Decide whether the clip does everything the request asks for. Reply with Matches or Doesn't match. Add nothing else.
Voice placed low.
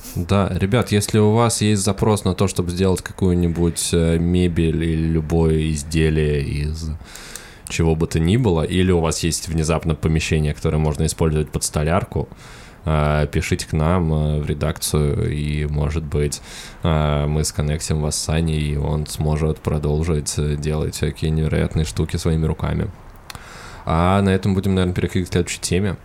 Matches